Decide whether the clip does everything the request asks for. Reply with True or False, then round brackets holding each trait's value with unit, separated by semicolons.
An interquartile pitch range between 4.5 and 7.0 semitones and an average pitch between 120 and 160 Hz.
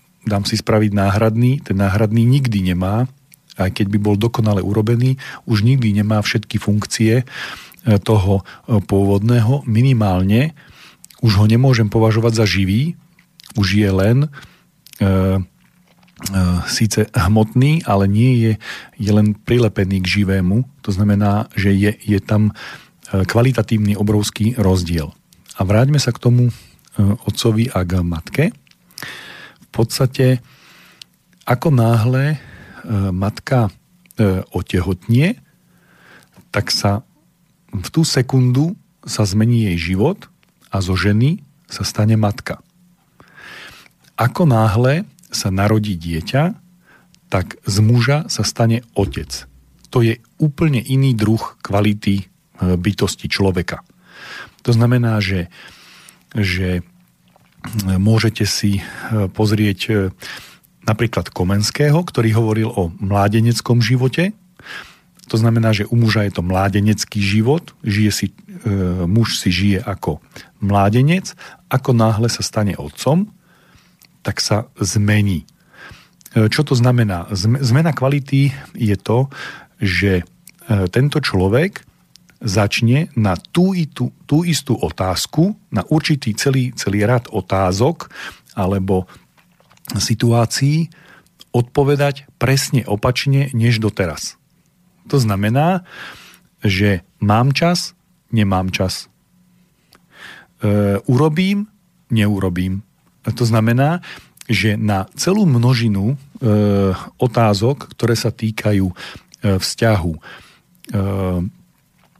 False (5.0 semitones; 110 Hz)